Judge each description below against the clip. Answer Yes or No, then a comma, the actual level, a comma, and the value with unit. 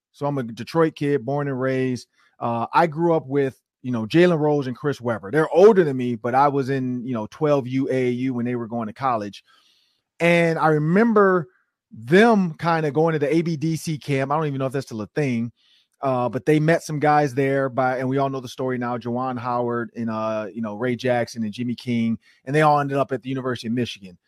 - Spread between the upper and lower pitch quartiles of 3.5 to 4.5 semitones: Yes, average, 3.8 semitones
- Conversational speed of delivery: No, fast, 230 wpm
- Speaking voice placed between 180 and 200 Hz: No, low, 135 Hz